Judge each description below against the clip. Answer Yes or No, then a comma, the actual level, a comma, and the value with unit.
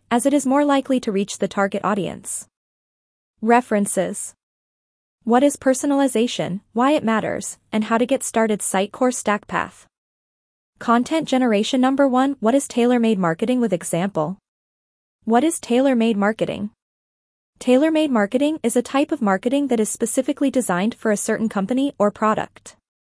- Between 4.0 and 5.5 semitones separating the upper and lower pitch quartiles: Yes, average, 4.3 semitones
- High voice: Yes, high, 235 Hz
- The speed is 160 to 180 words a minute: No, average, 145 wpm